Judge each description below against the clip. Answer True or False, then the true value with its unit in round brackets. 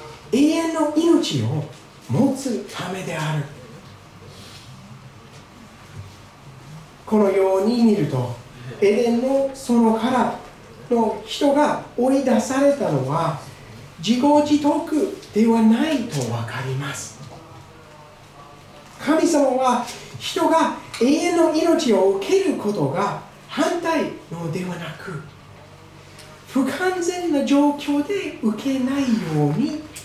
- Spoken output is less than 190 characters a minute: True (180 characters per minute)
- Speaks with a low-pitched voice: False (225 Hz)